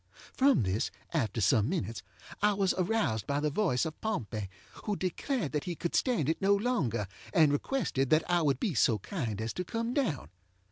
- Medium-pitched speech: Yes, medium, 160 Hz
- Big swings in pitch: Yes, wide, 9.0 semitones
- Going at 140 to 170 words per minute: No, average, 190 wpm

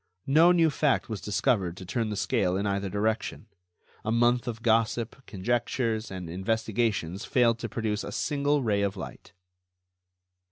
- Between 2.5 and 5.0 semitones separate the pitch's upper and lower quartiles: Yes, average, 3.3 semitones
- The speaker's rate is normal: Yes, average, 155 wpm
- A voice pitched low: Yes, low, 110 Hz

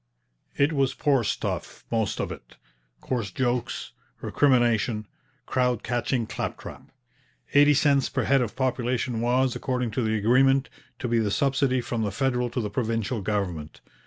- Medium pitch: No, low, 125 Hz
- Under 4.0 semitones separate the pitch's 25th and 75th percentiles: Yes, average, 2.9 semitones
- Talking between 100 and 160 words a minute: Yes, average, 150 wpm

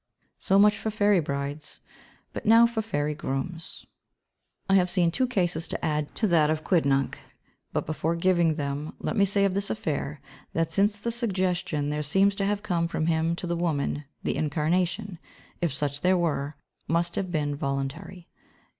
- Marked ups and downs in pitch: No, average, 4.6 semitones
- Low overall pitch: No, medium, 170 Hz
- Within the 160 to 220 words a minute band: Yes, average, 170 wpm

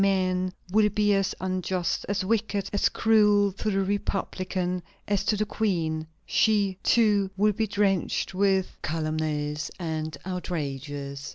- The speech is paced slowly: Yes, slow, 130 wpm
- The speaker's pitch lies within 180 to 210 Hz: Yes, high, 190 Hz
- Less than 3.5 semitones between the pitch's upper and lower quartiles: No, average, 3.8 semitones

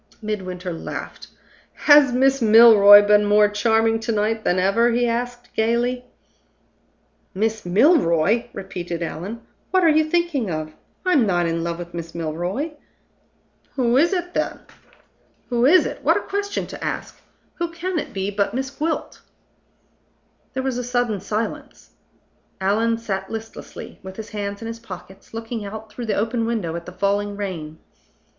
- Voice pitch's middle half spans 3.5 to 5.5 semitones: Yes, average, 4.1 semitones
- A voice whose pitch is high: Yes, high, 220 Hz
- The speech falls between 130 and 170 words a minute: Yes, average, 155 wpm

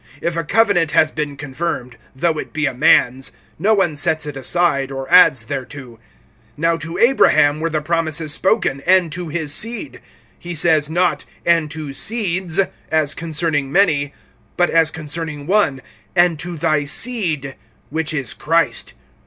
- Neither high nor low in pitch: Yes, medium, 160 Hz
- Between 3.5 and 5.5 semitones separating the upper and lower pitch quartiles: No, average, 3.0 semitones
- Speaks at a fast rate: No, average, 155 wpm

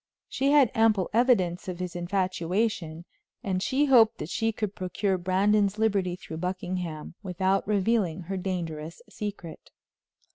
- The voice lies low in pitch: No, high, 190 Hz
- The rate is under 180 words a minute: Yes, slow, 135 wpm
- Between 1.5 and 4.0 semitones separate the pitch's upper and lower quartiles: Yes, average, 3.2 semitones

